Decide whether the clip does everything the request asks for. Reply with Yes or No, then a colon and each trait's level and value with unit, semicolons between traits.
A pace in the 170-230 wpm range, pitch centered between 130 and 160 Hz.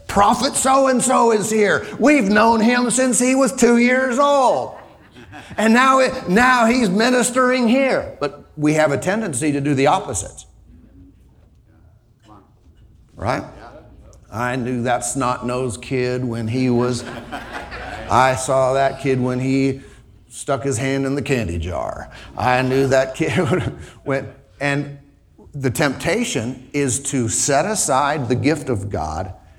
No: average, 140 wpm; low, 135 Hz